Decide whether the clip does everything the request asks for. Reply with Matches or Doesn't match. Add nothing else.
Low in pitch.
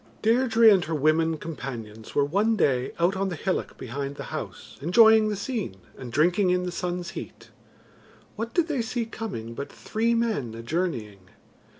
Doesn't match